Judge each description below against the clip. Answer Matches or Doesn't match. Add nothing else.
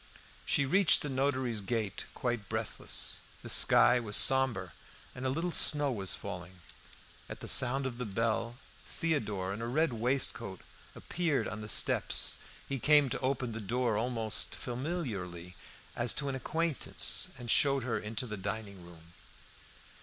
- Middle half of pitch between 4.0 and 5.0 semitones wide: Matches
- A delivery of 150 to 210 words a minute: Matches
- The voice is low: Matches